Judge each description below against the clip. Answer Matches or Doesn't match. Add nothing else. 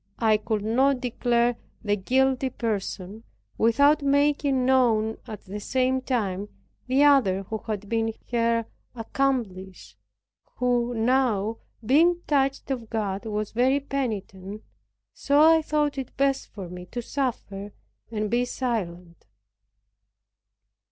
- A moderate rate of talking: Doesn't match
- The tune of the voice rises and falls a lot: Doesn't match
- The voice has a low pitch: Doesn't match